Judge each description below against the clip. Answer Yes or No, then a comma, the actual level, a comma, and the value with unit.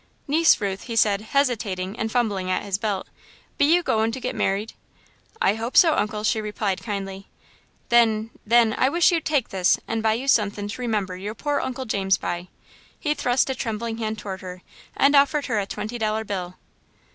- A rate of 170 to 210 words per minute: Yes, average, 195 wpm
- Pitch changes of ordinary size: Yes, average, 3.6 semitones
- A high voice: Yes, high, 220 Hz